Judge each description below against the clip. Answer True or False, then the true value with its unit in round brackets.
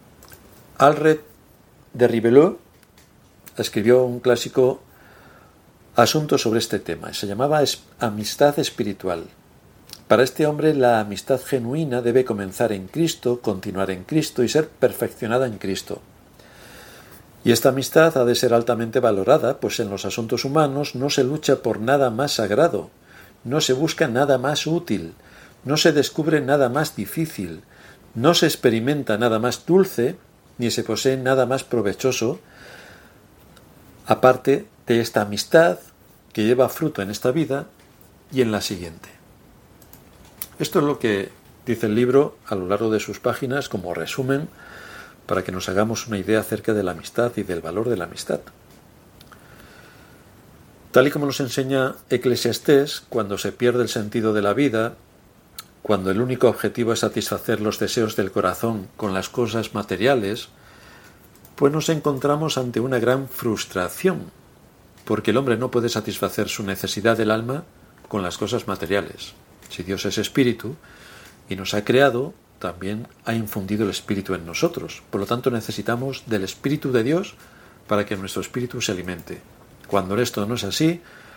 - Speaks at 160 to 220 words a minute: False (150 wpm)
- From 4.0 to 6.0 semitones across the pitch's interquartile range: True (4.6 semitones)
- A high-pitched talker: False (120 Hz)